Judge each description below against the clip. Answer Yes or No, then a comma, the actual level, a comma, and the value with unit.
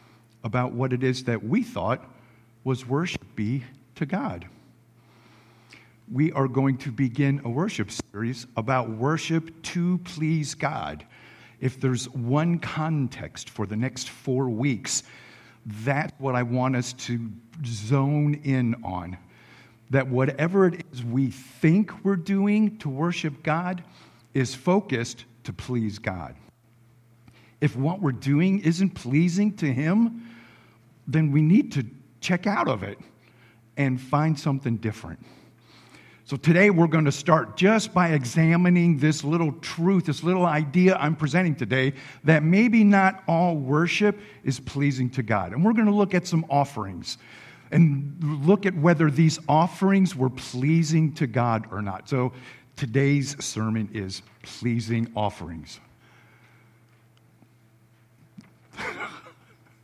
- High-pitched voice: No, low, 135 Hz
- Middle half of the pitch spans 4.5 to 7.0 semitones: Yes, average, 5.3 semitones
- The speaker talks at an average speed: No, slow, 130 wpm